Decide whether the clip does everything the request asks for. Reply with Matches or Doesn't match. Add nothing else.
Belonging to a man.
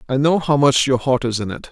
Matches